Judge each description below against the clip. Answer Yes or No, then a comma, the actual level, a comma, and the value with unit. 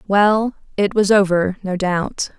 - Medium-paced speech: Yes, average, 150 wpm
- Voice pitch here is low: No, high, 195 Hz